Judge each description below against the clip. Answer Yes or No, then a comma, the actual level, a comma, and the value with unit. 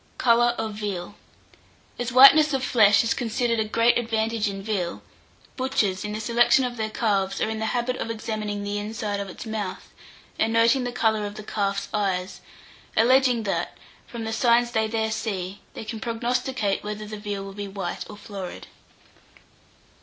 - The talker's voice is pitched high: Yes, high, 220 Hz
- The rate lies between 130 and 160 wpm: No, average, 175 wpm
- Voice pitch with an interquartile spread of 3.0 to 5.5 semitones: No, narrow, 2.5 semitones